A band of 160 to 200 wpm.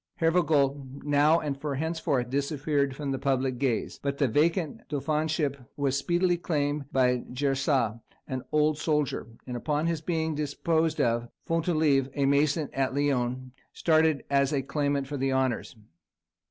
No: average, 140 wpm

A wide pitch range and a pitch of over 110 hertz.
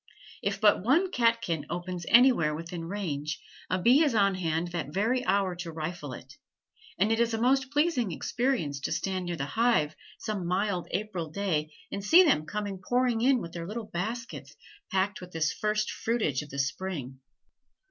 Yes: wide, 5.8 semitones; high, 190 Hz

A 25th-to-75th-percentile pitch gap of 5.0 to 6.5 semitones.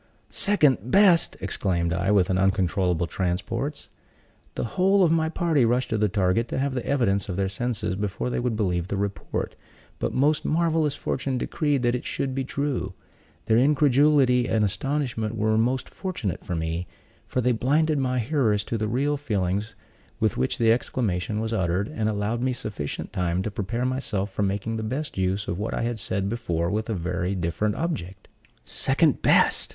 Yes: wide, 5.5 semitones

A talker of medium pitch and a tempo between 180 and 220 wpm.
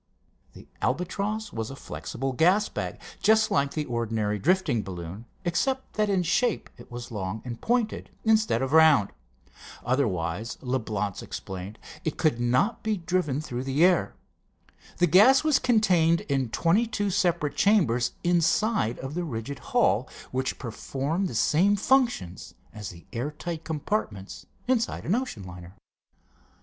No: medium, 150 Hz; average, 145 wpm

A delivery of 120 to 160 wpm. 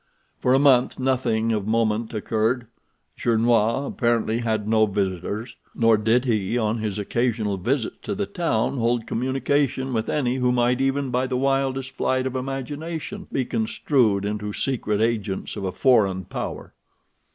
Yes: average, 150 wpm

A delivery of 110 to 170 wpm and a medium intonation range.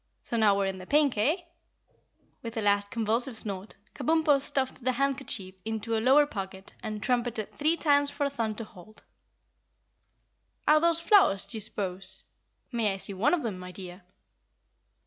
No: average, 165 wpm; wide, 5.7 semitones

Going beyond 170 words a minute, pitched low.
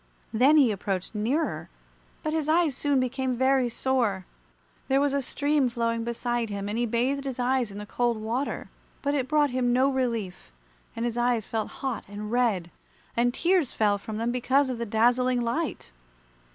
No: average, 180 wpm; high, 245 Hz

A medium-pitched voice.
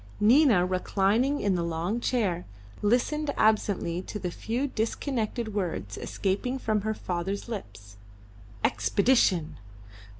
No: high, 205 Hz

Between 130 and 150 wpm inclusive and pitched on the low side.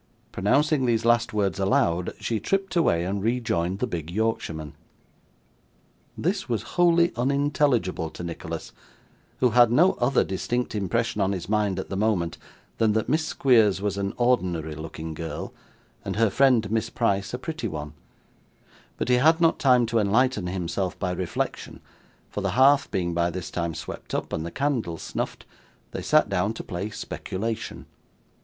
No: average, 165 wpm; low, 110 Hz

